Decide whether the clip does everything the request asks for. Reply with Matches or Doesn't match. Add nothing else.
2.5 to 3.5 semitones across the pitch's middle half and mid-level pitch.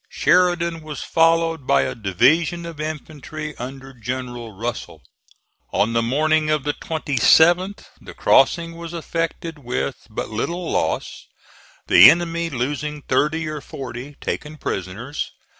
Doesn't match